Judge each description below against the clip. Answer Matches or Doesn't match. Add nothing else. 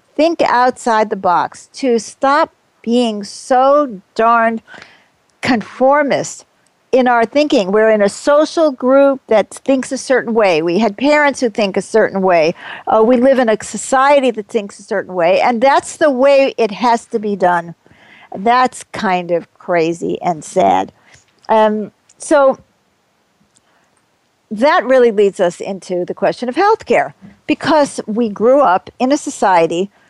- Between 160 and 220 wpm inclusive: Doesn't match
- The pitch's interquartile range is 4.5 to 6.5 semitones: Matches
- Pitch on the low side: Doesn't match